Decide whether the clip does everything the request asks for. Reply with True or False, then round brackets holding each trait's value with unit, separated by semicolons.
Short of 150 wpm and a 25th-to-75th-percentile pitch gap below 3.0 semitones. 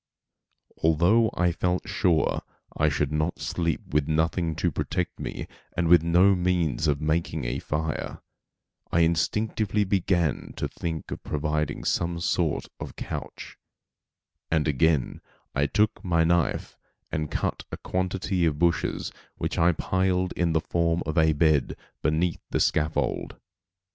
True (140 wpm; 2.4 semitones)